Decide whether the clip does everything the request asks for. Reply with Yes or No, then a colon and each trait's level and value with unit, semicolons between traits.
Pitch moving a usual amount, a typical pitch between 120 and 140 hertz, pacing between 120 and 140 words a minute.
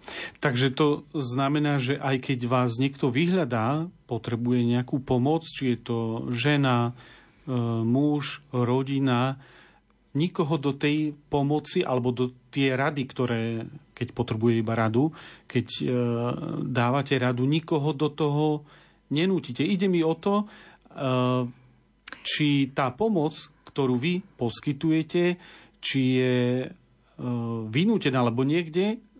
No: average, 3.7 semitones; low, 135 Hz; slow, 110 wpm